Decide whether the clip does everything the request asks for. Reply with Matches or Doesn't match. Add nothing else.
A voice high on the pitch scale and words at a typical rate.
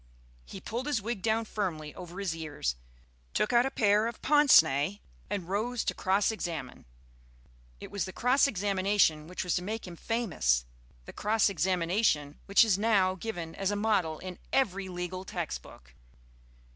Matches